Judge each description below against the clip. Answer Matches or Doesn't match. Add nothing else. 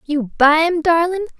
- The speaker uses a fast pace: Doesn't match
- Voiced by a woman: Matches